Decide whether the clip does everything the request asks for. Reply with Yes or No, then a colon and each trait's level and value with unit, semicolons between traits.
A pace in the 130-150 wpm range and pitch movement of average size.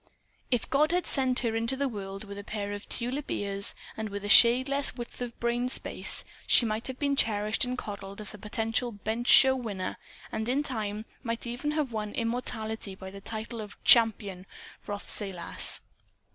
No: average, 185 wpm; average, 3.4 semitones